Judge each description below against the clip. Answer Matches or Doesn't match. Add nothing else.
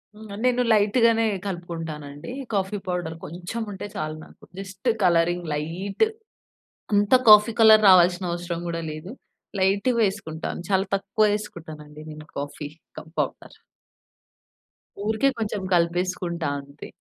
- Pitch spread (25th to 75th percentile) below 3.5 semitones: Doesn't match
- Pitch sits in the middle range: Matches